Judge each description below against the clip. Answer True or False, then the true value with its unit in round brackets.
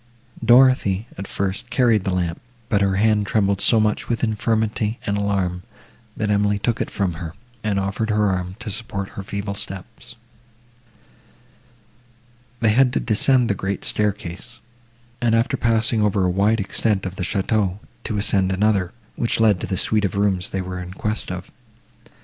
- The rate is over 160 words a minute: True (170 wpm)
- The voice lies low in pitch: True (100 Hz)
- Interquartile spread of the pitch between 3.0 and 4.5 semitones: False (2.6 semitones)